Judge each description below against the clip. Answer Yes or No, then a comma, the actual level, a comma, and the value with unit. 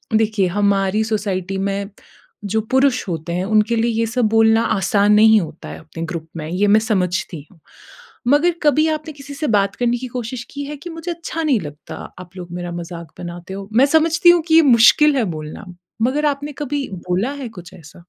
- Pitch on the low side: No, high, 220 Hz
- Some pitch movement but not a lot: No, wide, 7.2 semitones